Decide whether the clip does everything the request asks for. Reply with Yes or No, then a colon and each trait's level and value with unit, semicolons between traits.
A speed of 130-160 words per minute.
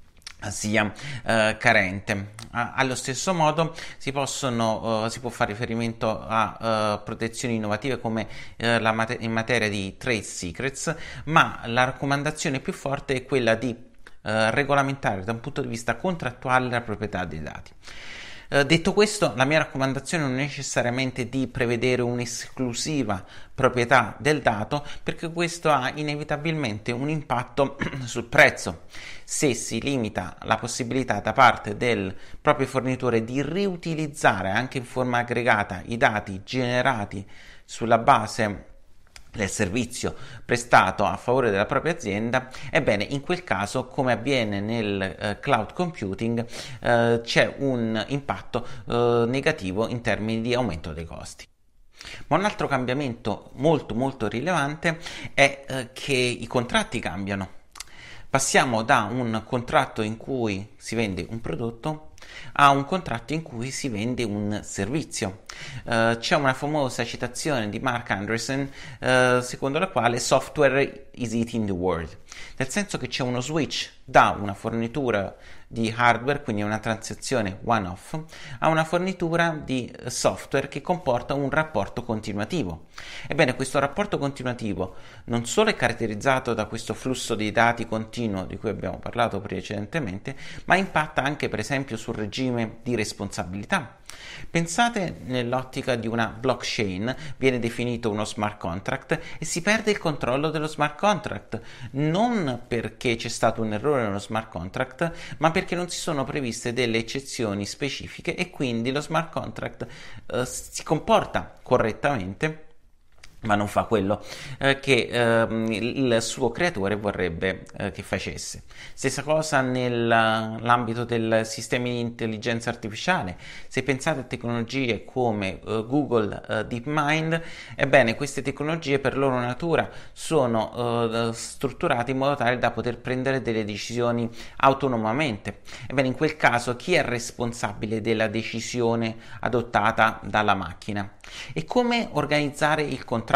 Yes: average, 140 wpm